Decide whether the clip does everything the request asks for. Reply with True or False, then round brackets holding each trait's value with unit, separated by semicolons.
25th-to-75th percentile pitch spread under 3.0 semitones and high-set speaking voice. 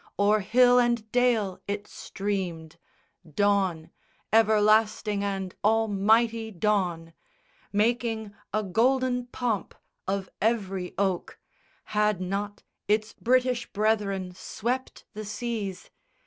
True (2.6 semitones; 210 Hz)